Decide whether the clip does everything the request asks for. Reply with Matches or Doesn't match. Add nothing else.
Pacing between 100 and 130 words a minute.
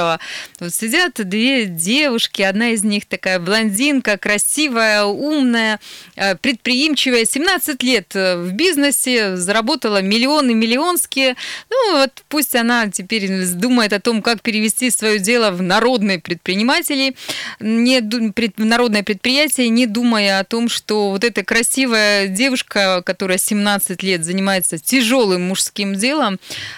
Matches